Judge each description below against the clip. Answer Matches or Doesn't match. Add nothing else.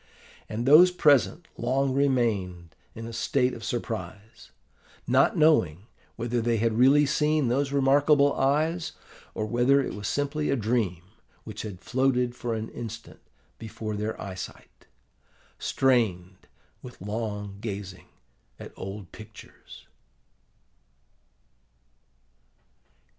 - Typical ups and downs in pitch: Matches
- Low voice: Matches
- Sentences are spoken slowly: Matches